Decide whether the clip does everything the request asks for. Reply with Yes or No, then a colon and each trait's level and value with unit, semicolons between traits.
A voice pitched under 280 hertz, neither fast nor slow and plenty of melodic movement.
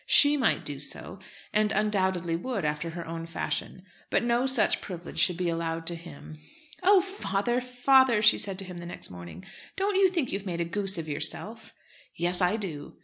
Yes: medium, 185 Hz; average, 195 wpm; wide, 6.2 semitones